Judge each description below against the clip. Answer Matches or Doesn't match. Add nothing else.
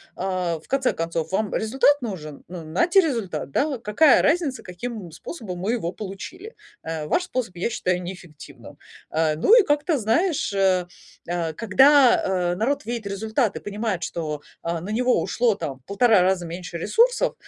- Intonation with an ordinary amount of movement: Doesn't match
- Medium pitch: Doesn't match